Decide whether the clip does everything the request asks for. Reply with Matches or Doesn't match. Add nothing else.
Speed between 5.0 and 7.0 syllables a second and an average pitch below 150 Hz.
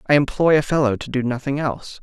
Matches